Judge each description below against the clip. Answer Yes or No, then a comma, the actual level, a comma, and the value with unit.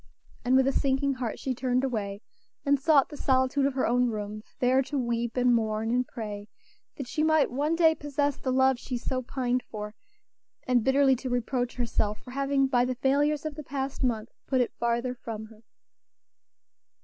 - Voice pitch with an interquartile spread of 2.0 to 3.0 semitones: Yes, narrow, 2.4 semitones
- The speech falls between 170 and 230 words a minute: Yes, average, 190 wpm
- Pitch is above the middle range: Yes, very high, 255 Hz